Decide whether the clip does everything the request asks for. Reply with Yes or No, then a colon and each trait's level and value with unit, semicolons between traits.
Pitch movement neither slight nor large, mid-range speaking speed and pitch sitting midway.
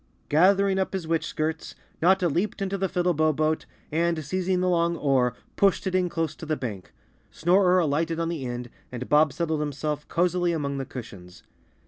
Yes: average, 3.6 semitones; average, 180 wpm; medium, 160 Hz